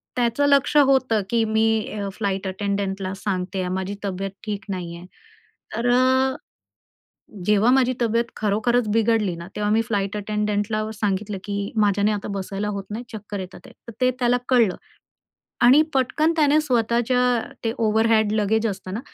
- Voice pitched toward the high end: Yes, high, 215 Hz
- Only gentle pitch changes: No, average, 3.2 semitones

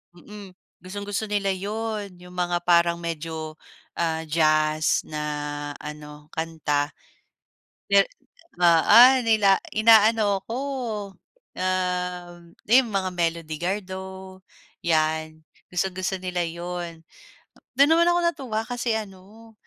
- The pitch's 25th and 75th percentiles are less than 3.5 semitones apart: No, average, 4.0 semitones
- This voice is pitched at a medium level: Yes, medium, 180 Hz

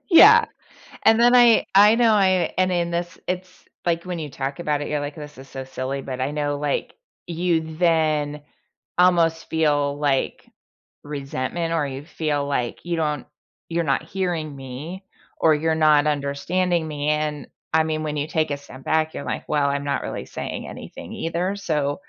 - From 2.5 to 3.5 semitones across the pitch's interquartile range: Yes, average, 3.2 semitones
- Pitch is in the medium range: Yes, medium, 155 Hz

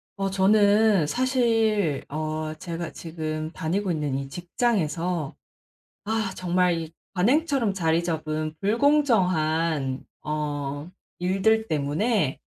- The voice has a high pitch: No, medium, 175 Hz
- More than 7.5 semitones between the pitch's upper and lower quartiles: No, average, 5.2 semitones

